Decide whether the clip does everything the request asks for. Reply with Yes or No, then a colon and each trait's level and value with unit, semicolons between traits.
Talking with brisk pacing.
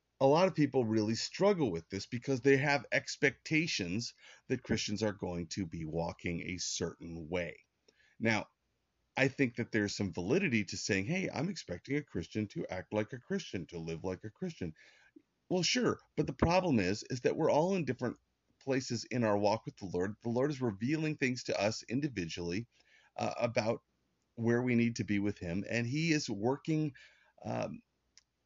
No: average, 185 wpm